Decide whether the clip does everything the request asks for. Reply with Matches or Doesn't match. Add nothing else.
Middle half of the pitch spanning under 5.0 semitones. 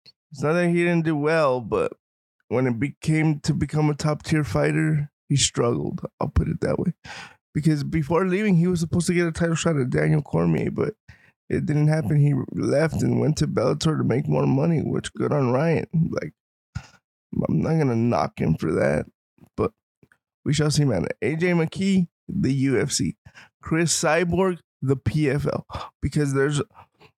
Matches